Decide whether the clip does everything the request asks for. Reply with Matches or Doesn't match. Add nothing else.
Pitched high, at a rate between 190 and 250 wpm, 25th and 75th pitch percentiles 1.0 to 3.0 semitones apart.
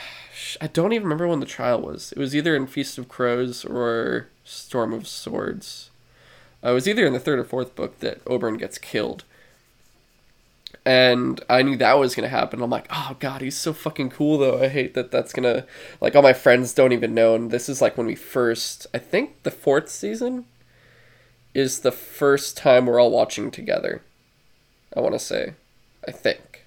Doesn't match